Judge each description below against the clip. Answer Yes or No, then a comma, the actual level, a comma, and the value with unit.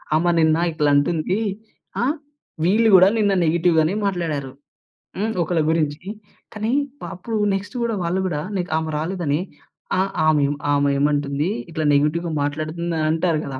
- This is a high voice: No, medium, 165 Hz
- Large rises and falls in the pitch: No, average, 3.6 semitones